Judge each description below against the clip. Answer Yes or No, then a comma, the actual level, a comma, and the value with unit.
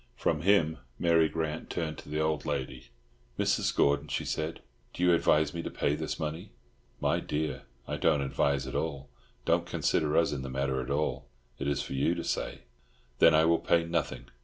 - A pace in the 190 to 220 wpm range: Yes, average, 195 wpm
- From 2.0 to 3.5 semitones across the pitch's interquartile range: Yes, narrow, 2.5 semitones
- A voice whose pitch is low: Yes, very low, 75 Hz